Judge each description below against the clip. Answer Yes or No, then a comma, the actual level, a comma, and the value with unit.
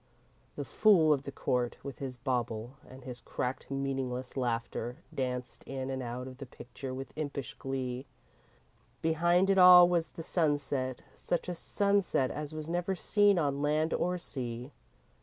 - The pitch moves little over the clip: No, average, 4.4 semitones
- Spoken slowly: No, average, 160 wpm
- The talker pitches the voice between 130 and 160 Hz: Yes, low, 135 Hz